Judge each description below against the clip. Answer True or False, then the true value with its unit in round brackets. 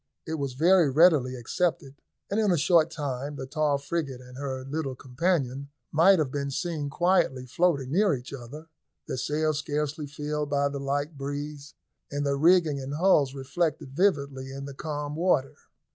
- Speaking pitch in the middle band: True (145 Hz)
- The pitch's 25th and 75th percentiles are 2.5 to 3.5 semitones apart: True (2.8 semitones)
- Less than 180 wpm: True (170 wpm)